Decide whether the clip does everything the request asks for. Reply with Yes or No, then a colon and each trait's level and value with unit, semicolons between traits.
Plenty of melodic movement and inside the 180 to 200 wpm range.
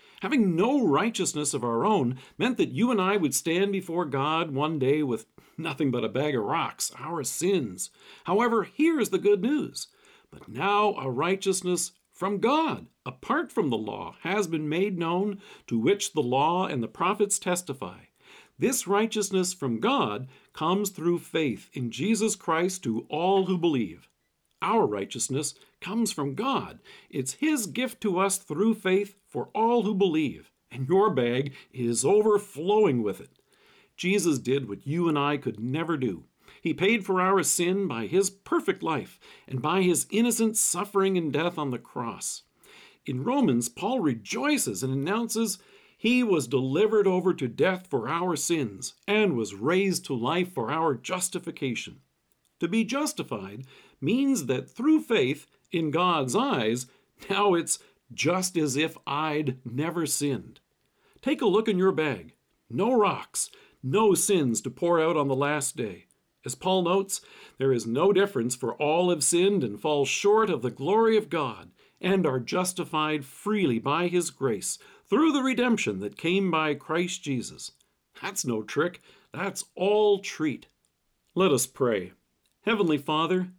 No: wide, 6.2 semitones; average, 160 wpm